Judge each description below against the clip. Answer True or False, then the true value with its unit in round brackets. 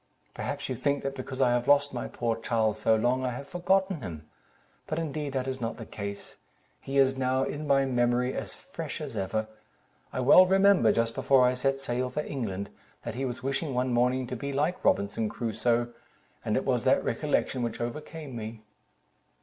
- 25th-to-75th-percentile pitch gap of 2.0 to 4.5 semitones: True (2.9 semitones)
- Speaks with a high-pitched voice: False (130 Hz)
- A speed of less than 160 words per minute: False (195 wpm)